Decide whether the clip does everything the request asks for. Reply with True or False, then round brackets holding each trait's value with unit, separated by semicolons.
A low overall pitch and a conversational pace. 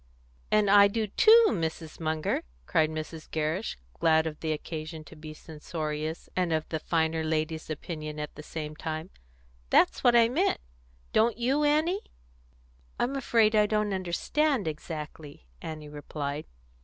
False (160 Hz; 145 wpm)